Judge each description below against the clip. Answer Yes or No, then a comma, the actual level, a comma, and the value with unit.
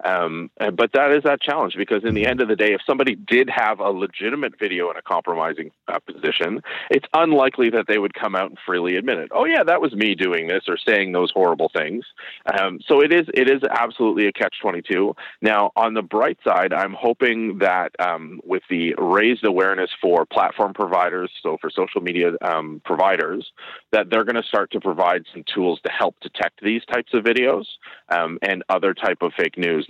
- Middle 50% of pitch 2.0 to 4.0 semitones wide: No, average, 4.7 semitones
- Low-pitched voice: Yes, low, 105 Hz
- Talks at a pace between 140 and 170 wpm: No, fast, 205 wpm